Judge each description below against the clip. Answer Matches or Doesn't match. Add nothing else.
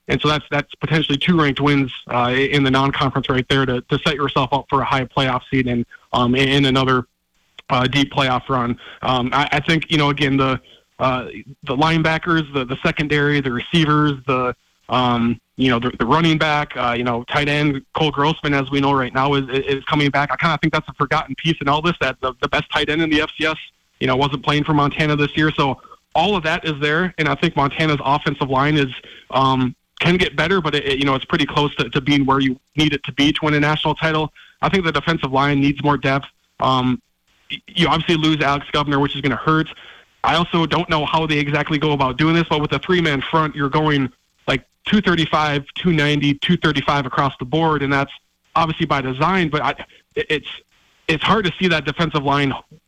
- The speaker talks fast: Matches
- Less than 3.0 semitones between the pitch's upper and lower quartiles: Matches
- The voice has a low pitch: Doesn't match